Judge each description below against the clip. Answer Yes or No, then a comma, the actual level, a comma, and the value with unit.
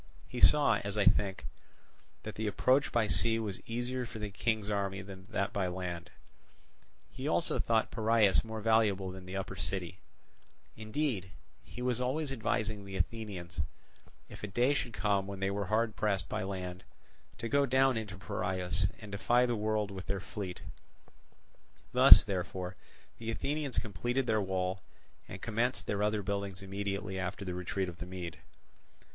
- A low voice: Yes, low, 100 Hz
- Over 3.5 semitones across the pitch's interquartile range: No, average, 3.2 semitones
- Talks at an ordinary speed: Yes, average, 165 wpm